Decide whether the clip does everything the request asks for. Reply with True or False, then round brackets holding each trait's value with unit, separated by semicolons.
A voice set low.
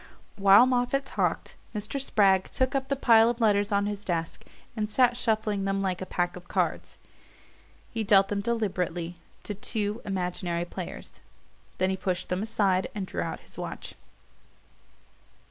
False (205 Hz)